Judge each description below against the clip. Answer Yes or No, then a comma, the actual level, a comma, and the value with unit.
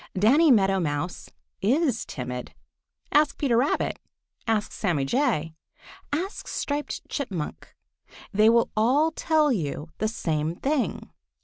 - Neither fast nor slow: No, slow, 115 wpm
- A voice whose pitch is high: Yes, high, 225 Hz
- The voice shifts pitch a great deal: Yes, wide, 8.9 semitones